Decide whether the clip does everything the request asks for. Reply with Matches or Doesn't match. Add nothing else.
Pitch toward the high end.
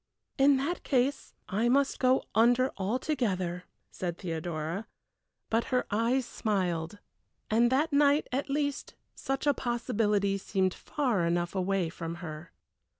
Matches